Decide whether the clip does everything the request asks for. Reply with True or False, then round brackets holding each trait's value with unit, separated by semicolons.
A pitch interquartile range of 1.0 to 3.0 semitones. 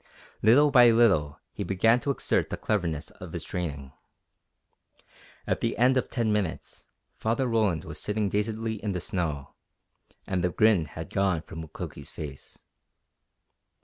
False (5.5 semitones)